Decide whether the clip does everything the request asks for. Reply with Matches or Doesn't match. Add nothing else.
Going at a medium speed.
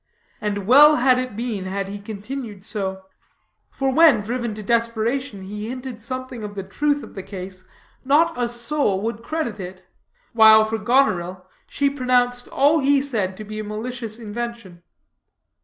Matches